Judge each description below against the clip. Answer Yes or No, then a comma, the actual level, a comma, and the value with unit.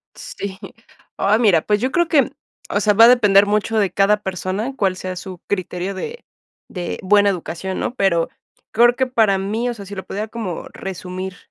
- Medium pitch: No, high, 200 Hz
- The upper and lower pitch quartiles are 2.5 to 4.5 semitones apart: Yes, average, 2.9 semitones